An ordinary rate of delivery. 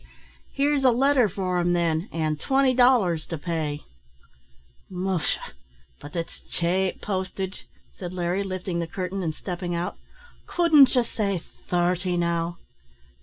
No: slow, 130 wpm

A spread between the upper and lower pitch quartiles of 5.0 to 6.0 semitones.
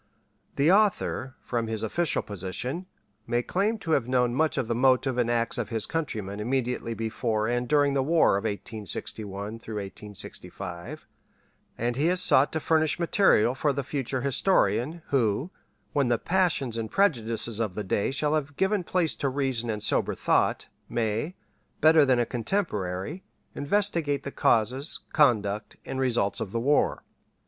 Yes: average, 5.3 semitones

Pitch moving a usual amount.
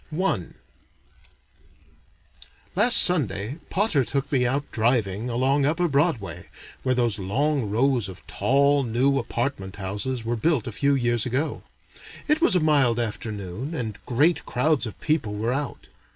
Yes: average, 4.5 semitones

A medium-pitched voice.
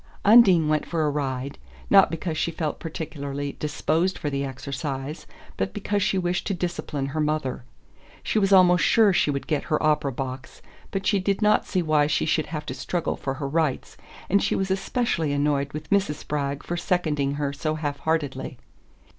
Yes: medium, 155 Hz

